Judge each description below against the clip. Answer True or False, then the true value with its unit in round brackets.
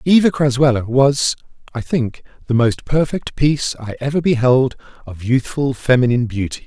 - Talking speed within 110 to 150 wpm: True (145 wpm)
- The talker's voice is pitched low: True (130 Hz)